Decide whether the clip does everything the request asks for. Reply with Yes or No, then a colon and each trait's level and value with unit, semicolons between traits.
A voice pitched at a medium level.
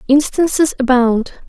No: very high, 275 Hz